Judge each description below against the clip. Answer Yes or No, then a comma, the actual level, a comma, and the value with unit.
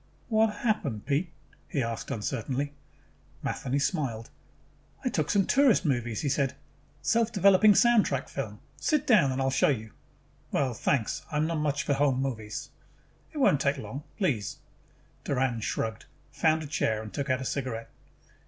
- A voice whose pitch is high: No, medium, 140 Hz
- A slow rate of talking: No, average, 165 wpm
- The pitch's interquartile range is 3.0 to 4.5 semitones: No, average, 5.2 semitones